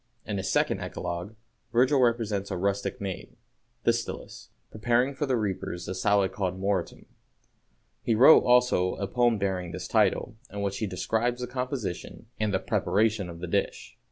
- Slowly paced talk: No, average, 155 wpm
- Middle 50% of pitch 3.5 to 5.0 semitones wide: Yes, average, 4.3 semitones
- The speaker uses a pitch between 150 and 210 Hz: No, low, 105 Hz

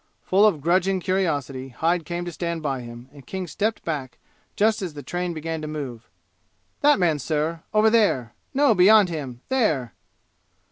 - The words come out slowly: No, average, 170 wpm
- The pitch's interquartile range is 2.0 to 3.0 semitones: No, average, 5.2 semitones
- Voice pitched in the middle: Yes, medium, 165 Hz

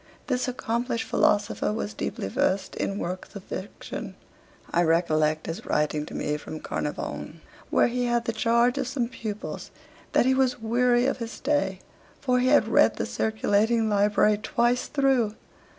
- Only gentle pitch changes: No, average, 3.7 semitones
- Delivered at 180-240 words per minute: No, average, 160 wpm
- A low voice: No, high, 230 Hz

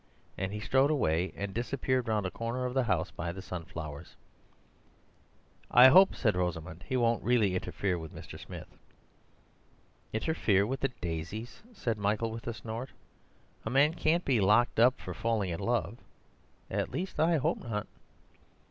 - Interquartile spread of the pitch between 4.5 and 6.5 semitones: Yes, average, 5.2 semitones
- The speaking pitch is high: No, low, 115 Hz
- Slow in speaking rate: No, average, 155 wpm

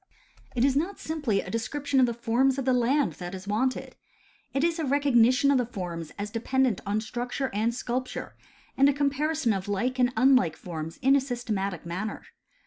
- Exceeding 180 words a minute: Yes, average, 195 wpm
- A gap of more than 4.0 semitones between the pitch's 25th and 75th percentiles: Yes, average, 4.6 semitones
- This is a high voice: Yes, high, 245 Hz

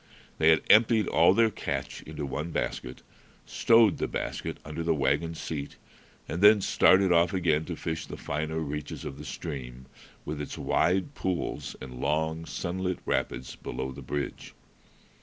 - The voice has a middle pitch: No, very low, 80 Hz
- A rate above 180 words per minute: No, average, 155 wpm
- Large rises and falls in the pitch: No, average, 3.9 semitones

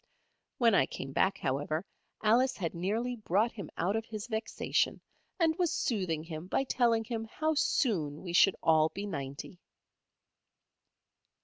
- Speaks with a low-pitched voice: No, high, 200 Hz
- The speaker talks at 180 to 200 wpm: No, average, 145 wpm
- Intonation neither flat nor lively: No, wide, 6.2 semitones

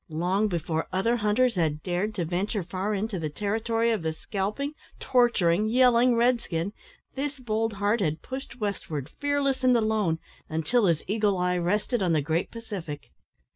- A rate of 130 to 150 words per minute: No, average, 165 wpm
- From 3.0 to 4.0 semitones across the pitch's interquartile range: No, average, 5.1 semitones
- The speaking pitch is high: Yes, high, 205 Hz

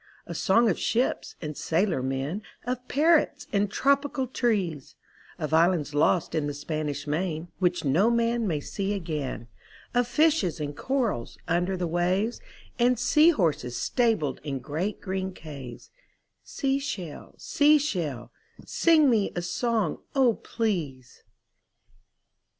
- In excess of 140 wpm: No, slow, 135 wpm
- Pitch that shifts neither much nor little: No, wide, 7.8 semitones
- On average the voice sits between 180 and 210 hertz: Yes, medium, 185 Hz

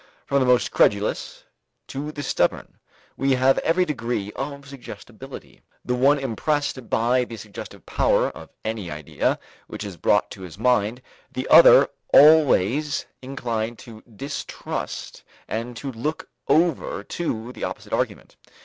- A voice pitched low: Yes, low, 125 Hz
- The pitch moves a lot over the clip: No, average, 4.1 semitones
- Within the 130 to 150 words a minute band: Yes, average, 140 wpm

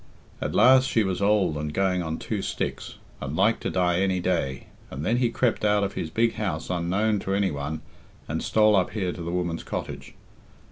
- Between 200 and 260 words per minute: Yes, fast, 205 wpm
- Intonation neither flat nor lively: Yes, average, 3.9 semitones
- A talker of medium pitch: No, very low, 95 Hz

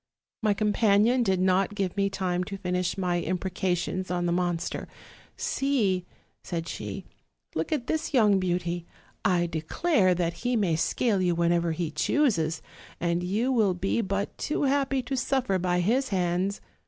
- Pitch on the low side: No, medium, 185 Hz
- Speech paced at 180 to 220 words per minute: No, average, 155 wpm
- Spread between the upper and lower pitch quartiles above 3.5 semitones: Yes, average, 4.1 semitones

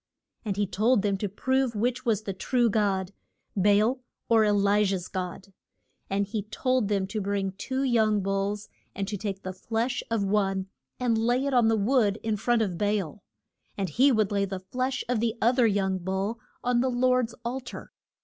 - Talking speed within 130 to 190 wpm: No, fast, 205 wpm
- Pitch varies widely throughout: No, average, 3.5 semitones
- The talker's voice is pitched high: Yes, high, 210 Hz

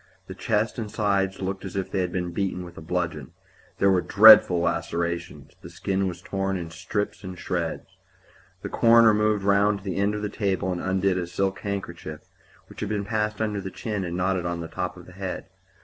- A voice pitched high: No, very low, 95 Hz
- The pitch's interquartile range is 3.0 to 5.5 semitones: No, narrow, 2.4 semitones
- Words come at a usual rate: No, fast, 210 wpm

